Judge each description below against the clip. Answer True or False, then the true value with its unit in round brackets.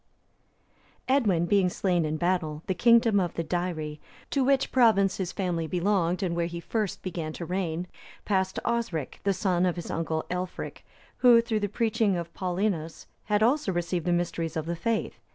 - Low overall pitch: False (180 Hz)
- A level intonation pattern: False (3.7 semitones)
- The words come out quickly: False (185 wpm)